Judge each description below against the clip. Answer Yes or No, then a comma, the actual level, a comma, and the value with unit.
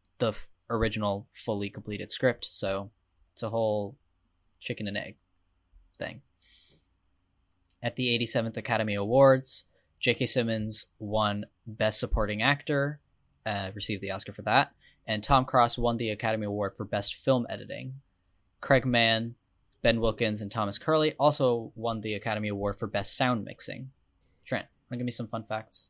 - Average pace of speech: Yes, average, 155 wpm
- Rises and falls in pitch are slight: No, average, 3.4 semitones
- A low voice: Yes, low, 110 Hz